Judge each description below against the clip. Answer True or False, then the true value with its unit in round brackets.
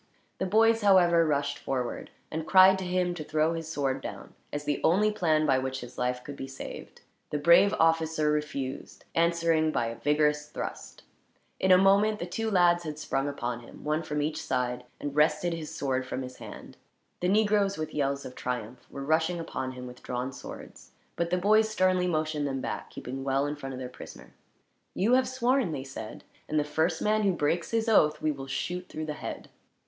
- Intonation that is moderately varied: True (4.8 semitones)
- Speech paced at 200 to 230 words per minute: True (205 wpm)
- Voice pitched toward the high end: False (155 Hz)